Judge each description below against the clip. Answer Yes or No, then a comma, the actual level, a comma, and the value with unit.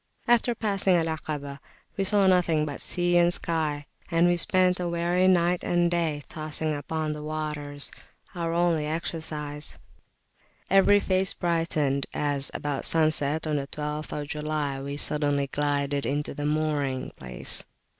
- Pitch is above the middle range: No, medium, 155 Hz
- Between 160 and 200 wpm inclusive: No, average, 145 wpm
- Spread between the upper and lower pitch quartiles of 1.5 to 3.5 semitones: Yes, average, 3.0 semitones